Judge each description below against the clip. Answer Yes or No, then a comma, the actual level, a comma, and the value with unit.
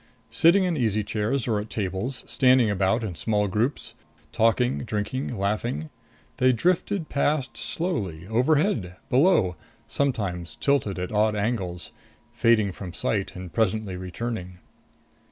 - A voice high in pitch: No, low, 110 Hz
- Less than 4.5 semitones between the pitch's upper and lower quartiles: No, average, 5.1 semitones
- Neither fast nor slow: No, slow, 125 wpm